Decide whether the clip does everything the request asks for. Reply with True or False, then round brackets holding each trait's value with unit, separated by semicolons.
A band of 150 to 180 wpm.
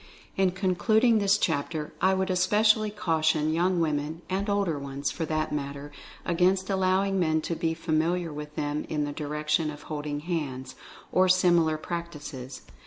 True (160 wpm)